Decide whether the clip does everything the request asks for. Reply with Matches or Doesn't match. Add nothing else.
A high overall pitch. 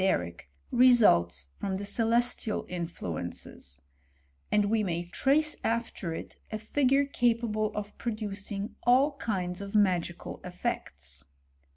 Matches